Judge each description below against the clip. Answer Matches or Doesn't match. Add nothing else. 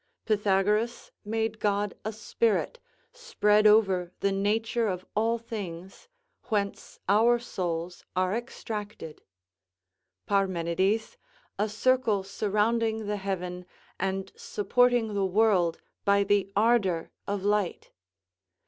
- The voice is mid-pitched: Doesn't match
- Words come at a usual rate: Doesn't match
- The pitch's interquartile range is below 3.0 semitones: Matches